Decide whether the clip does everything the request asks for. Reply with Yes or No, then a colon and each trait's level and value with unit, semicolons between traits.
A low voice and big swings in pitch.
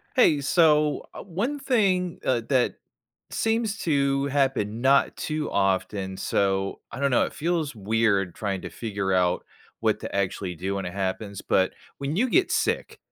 Yes: low, 130 Hz; wide, 8.2 semitones